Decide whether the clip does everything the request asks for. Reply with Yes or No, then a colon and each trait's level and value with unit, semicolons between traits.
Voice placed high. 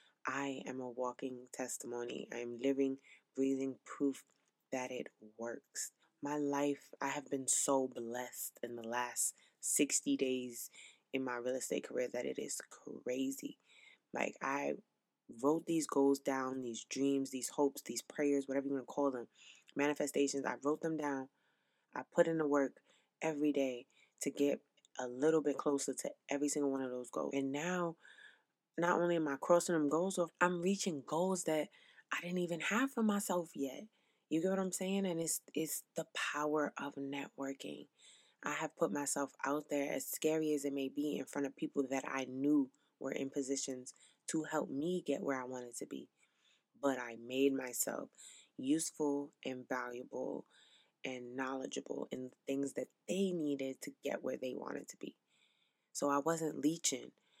No: medium, 140 Hz